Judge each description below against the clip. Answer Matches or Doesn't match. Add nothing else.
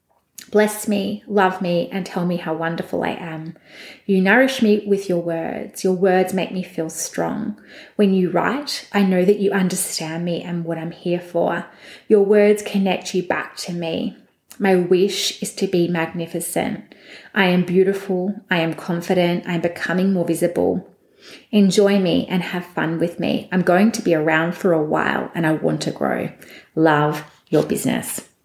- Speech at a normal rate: Matches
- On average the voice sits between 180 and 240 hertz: Matches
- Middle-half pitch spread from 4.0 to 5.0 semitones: Doesn't match